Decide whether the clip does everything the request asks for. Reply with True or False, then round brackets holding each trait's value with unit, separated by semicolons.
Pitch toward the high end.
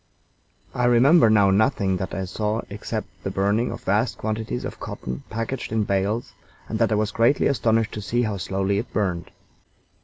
False (110 Hz)